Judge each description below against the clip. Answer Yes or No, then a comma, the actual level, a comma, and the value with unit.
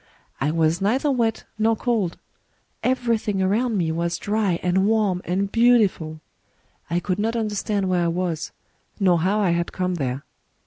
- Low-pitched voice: No, high, 190 Hz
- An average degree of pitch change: Yes, average, 4.2 semitones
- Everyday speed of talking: Yes, average, 160 wpm